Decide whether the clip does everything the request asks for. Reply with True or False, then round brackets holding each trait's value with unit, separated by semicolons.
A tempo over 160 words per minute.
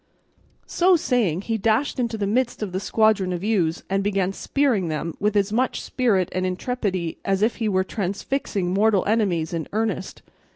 True (175 wpm)